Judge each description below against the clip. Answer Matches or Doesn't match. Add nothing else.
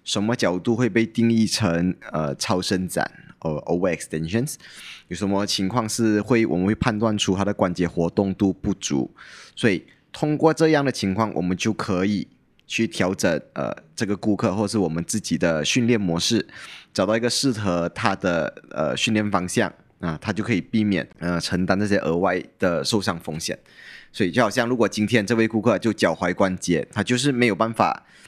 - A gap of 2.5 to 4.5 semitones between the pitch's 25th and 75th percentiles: Matches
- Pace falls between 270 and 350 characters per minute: Matches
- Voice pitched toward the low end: Matches